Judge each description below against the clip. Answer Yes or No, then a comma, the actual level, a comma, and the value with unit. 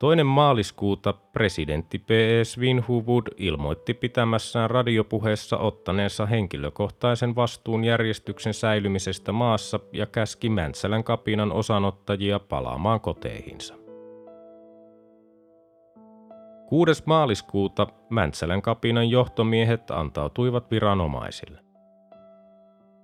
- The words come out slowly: Yes, slow, 75 wpm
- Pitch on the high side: No, low, 115 Hz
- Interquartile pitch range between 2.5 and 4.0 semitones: No, average, 4.7 semitones